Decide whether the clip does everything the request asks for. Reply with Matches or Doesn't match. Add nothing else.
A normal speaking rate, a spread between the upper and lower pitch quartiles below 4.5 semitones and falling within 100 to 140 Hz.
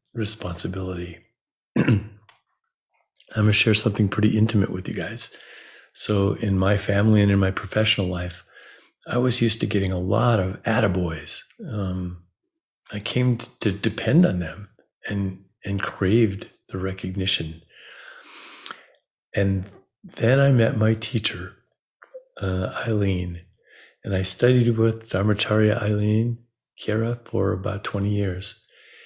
Doesn't match